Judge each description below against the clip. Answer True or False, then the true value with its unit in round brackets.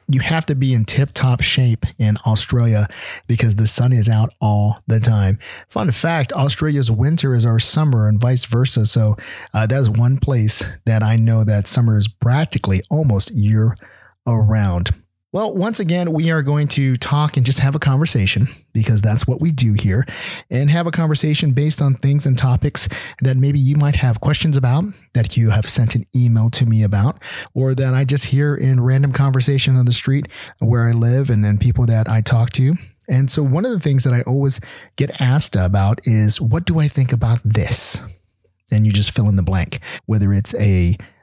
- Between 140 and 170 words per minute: False (200 wpm)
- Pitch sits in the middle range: False (125 Hz)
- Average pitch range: True (4.1 semitones)